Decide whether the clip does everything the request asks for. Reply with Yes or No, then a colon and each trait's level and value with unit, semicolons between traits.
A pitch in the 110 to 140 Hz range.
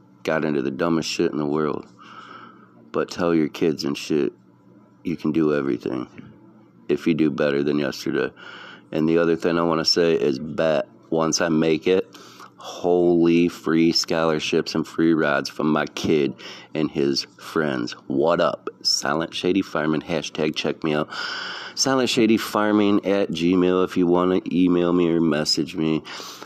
No: very low, 85 Hz